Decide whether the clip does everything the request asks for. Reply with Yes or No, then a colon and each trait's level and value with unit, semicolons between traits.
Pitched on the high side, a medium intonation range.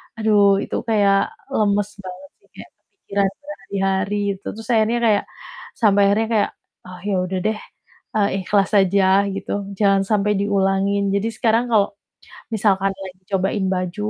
No: high, 200 Hz; narrow, 1.6 semitones